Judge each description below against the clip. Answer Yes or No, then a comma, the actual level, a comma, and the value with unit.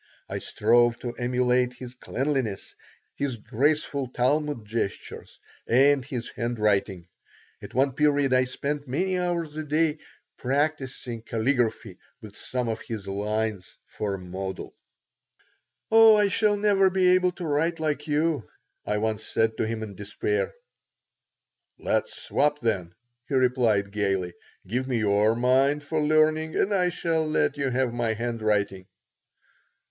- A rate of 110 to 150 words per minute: Yes, average, 140 wpm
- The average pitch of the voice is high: No, low, 125 Hz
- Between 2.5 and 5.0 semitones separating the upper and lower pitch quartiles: No, wide, 5.5 semitones